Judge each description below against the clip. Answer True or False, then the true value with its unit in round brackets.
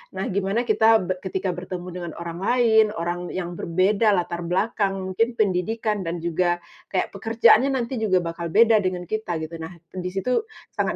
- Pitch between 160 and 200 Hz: True (190 Hz)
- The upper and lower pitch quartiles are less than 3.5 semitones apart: False (3.8 semitones)